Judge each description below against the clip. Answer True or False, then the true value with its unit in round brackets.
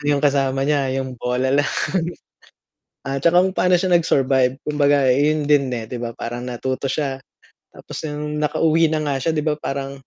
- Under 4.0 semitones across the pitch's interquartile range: True (2.4 semitones)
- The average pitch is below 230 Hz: True (140 Hz)